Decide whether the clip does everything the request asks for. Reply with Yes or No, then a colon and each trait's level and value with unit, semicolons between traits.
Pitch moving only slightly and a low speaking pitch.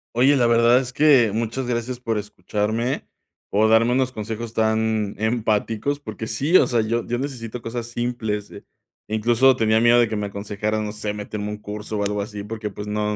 Yes: narrow, 2.2 semitones; low, 110 Hz